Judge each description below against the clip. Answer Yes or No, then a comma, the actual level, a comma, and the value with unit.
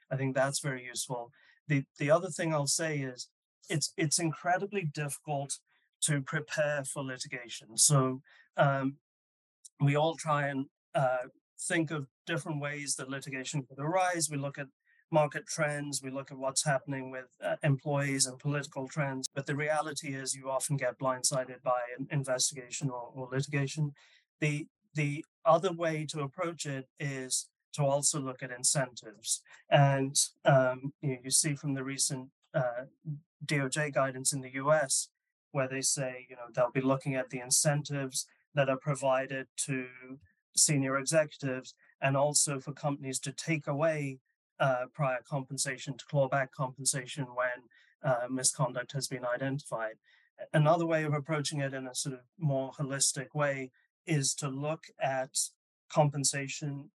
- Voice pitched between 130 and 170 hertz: Yes, medium, 140 Hz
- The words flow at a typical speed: Yes, average, 155 wpm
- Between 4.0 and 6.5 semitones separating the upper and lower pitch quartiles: No, narrow, 2.4 semitones